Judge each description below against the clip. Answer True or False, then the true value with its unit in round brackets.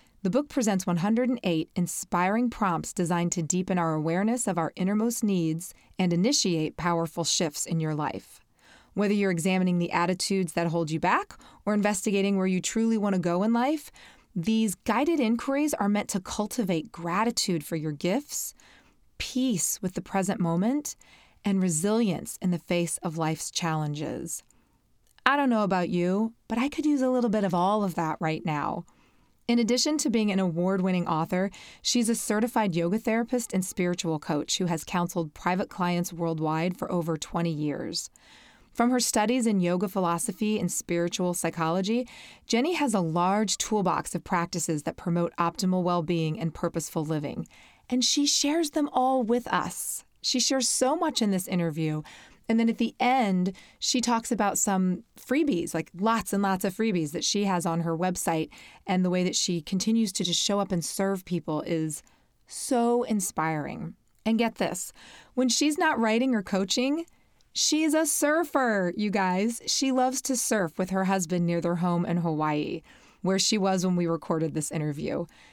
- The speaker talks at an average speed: True (175 wpm)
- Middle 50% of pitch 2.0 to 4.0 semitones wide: False (5.0 semitones)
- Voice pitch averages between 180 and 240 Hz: True (190 Hz)